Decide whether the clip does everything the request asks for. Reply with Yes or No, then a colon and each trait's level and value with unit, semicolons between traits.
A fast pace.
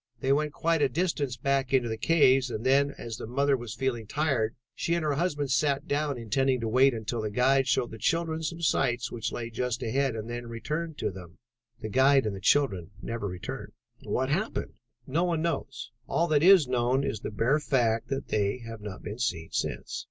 Yes: fast, 210 wpm